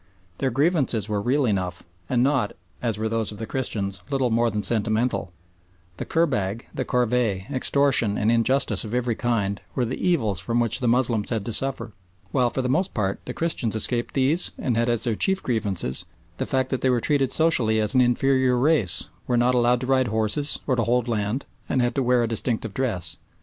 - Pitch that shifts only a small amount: No, average, 3.1 semitones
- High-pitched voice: No, low, 120 Hz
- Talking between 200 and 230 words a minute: Yes, fast, 205 wpm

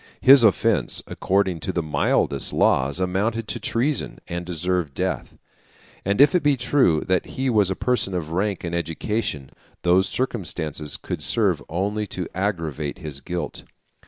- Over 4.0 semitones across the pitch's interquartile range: Yes, average, 4.6 semitones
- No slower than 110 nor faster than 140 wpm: No, average, 155 wpm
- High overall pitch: No, very low, 95 Hz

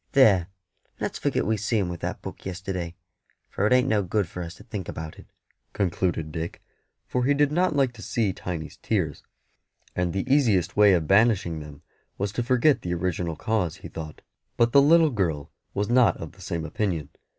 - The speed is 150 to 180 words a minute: No, average, 195 wpm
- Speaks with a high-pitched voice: No, very low, 95 Hz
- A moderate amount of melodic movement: No, wide, 5.7 semitones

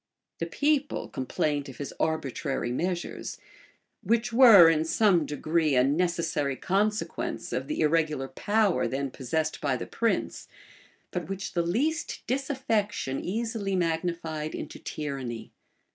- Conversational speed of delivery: No, slow, 125 wpm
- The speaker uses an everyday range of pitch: No, wide, 6.1 semitones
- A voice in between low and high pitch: Yes, medium, 165 Hz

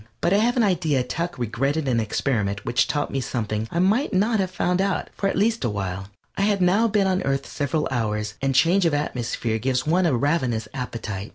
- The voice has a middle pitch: Yes, medium, 145 Hz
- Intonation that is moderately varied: No, wide, 8.1 semitones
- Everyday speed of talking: No, fast, 215 wpm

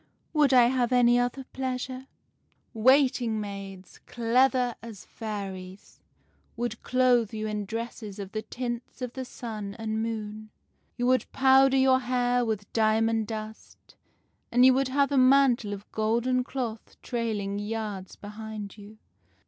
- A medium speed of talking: Yes, average, 150 wpm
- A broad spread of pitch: No, average, 3.0 semitones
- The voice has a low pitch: No, high, 230 Hz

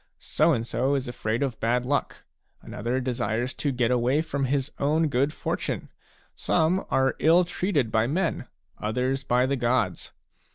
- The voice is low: Yes, low, 130 Hz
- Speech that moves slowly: No, average, 160 wpm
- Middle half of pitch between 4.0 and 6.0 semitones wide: No, average, 3.0 semitones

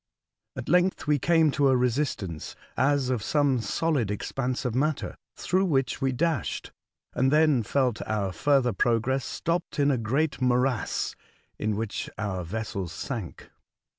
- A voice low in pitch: Yes, low, 130 Hz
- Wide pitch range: No, average, 4.6 semitones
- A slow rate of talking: No, average, 160 wpm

